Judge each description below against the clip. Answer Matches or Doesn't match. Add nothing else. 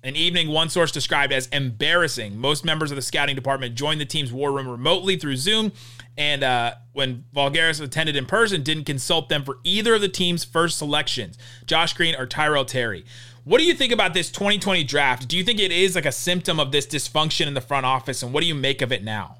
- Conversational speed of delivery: Doesn't match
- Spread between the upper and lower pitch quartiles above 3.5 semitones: Matches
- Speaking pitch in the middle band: Matches